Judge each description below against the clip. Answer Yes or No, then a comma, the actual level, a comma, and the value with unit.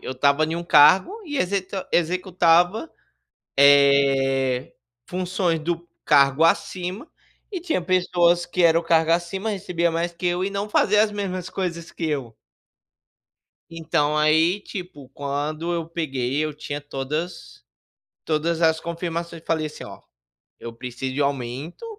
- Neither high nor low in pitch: Yes, medium, 165 Hz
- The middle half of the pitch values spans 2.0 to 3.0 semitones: No, average, 3.6 semitones